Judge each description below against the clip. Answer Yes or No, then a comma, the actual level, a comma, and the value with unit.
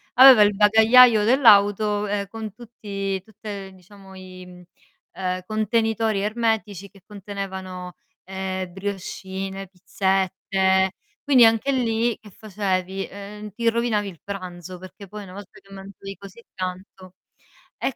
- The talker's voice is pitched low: No, high, 200 Hz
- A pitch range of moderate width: No, narrow, 2.3 semitones